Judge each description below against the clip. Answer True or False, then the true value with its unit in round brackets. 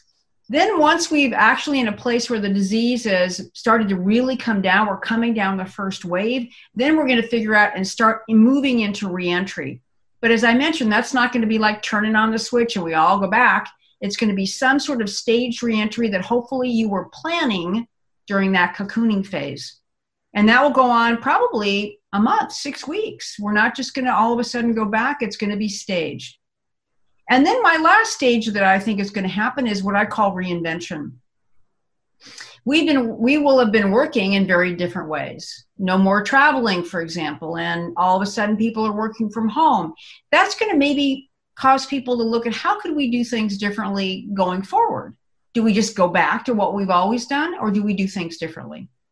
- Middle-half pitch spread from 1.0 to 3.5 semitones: False (4.1 semitones)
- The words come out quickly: True (210 wpm)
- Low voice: False (220 Hz)